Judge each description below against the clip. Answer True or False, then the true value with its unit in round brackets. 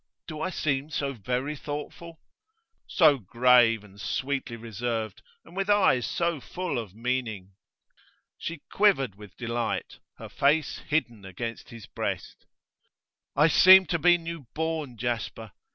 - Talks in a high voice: False (130 Hz)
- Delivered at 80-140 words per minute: True (135 wpm)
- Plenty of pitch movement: True (5.8 semitones)